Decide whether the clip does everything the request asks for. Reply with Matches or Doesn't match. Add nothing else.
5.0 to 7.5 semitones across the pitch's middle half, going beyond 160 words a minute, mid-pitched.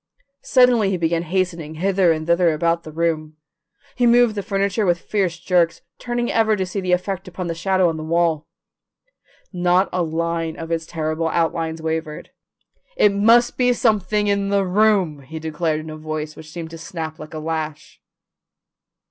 Doesn't match